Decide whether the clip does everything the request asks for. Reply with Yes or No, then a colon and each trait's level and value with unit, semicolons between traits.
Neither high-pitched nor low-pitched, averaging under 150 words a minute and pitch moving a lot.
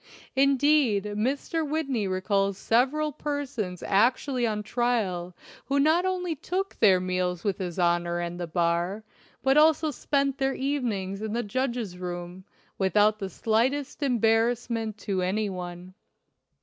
No: high, 220 Hz; slow, 135 wpm; wide, 6.6 semitones